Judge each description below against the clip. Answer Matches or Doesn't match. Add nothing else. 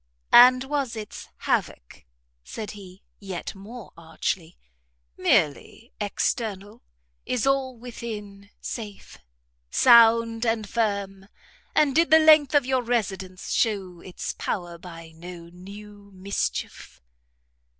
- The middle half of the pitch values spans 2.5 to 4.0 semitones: Doesn't match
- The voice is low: Doesn't match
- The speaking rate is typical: Doesn't match